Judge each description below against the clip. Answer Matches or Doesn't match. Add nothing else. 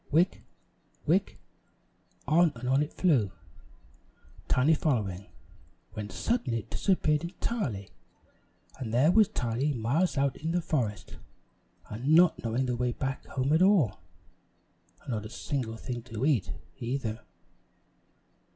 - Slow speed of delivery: Matches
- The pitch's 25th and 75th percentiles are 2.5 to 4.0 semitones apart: Doesn't match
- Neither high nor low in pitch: Doesn't match